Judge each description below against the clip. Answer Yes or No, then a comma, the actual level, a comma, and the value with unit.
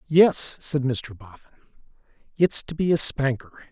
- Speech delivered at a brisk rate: No, average, 145 wpm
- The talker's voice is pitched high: No, medium, 140 Hz